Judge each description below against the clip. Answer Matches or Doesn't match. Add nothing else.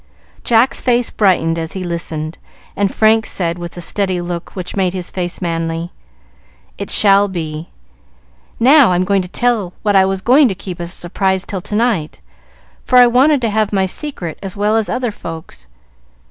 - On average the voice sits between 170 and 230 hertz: Matches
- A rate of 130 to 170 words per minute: Doesn't match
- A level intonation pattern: Doesn't match